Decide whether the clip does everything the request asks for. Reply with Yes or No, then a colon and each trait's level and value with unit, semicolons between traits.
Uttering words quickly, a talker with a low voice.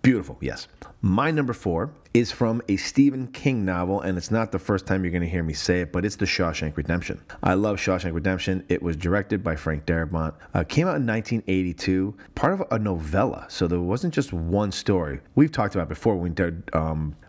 Yes: fast, 215 wpm; very low, 95 Hz